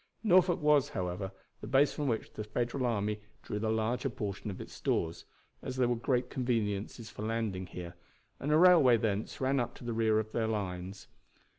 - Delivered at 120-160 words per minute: No, average, 190 wpm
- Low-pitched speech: Yes, low, 115 Hz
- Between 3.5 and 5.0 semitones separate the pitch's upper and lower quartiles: Yes, average, 3.8 semitones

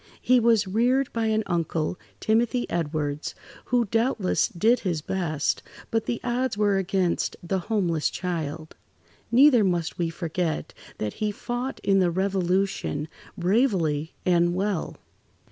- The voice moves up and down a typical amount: Yes, average, 4.9 semitones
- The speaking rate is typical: No, slow, 130 wpm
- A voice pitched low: No, high, 190 Hz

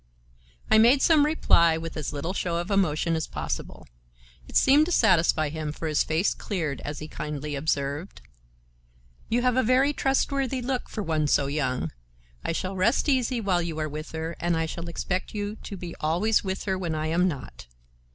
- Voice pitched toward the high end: No, medium, 170 Hz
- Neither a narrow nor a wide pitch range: No, wide, 5.9 semitones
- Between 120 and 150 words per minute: No, average, 190 wpm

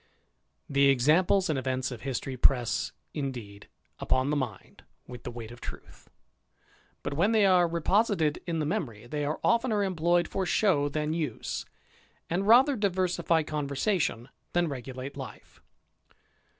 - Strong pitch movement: Yes, wide, 5.7 semitones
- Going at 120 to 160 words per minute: Yes, average, 140 wpm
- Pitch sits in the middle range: Yes, medium, 150 Hz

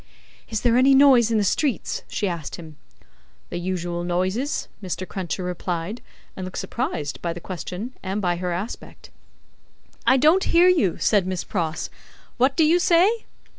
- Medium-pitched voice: No, high, 195 Hz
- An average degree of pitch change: No, wide, 6.8 semitones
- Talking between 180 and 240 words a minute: No, average, 165 wpm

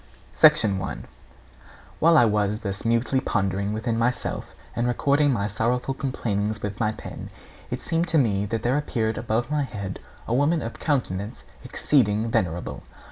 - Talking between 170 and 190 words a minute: No, average, 155 wpm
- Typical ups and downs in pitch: Yes, average, 4.2 semitones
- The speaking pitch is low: Yes, low, 115 Hz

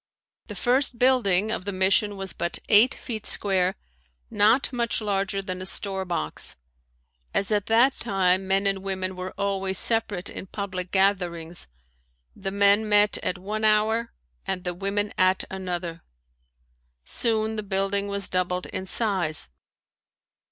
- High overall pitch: Yes, high, 195 Hz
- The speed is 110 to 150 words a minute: Yes, average, 140 wpm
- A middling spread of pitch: No, narrow, 2.3 semitones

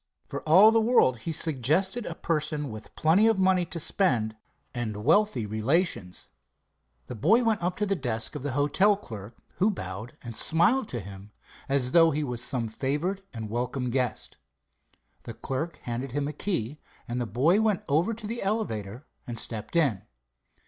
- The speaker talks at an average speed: Yes, average, 175 wpm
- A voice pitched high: No, medium, 145 Hz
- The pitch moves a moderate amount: No, wide, 8.0 semitones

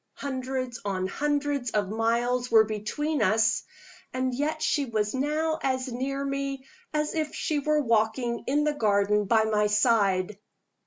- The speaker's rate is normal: Yes, average, 150 wpm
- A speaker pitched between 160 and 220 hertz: No, very high, 250 Hz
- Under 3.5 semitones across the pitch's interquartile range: No, average, 4.5 semitones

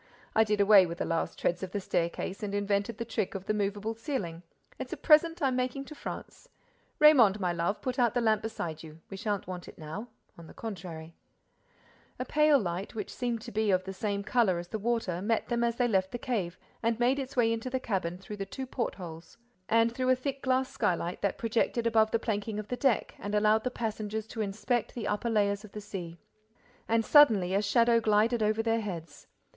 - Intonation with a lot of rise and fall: No, average, 3.6 semitones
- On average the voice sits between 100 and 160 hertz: No, high, 215 Hz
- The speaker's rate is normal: No, fast, 215 wpm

